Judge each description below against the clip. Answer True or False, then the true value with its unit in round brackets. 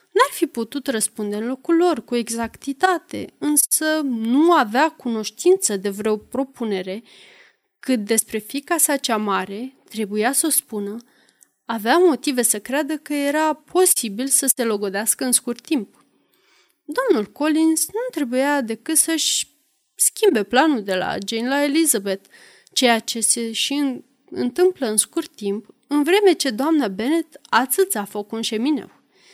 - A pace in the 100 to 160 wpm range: True (145 wpm)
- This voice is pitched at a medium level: False (260 Hz)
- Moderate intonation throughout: False (5.7 semitones)